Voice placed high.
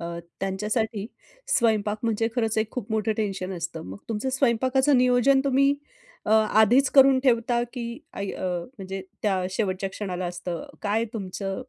Yes: high, 220 Hz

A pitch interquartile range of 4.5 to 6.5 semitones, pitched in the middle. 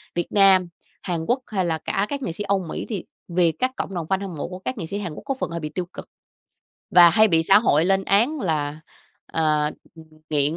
No: average, 3.7 semitones; medium, 180 Hz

